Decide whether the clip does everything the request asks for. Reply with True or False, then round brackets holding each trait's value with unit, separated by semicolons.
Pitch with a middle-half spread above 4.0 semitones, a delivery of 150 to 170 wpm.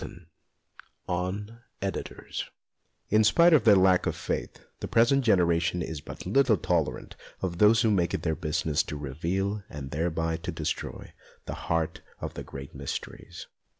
True (4.6 semitones; 155 wpm)